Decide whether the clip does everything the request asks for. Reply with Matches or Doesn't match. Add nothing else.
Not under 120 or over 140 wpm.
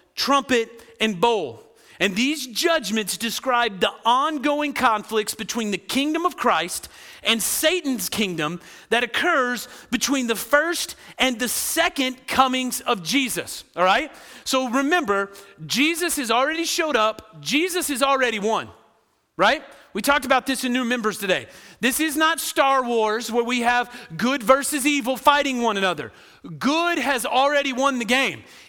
Doesn't match